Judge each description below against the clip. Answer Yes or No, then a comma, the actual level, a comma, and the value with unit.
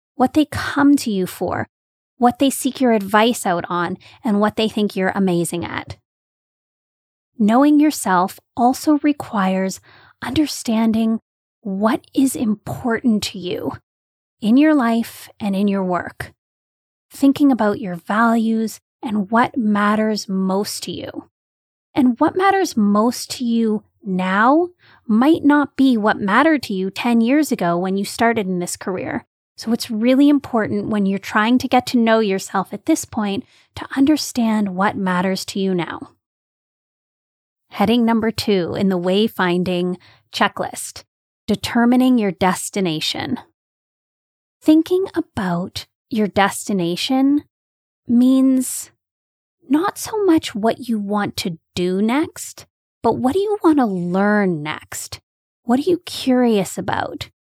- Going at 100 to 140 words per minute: Yes, slow, 135 wpm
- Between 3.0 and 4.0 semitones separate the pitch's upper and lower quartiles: No, average, 5.3 semitones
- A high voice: Yes, high, 225 Hz